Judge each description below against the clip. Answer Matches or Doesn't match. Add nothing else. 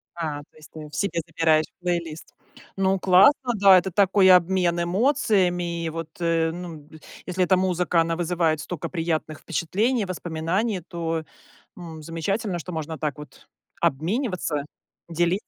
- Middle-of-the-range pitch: Matches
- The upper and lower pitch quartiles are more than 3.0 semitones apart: Doesn't match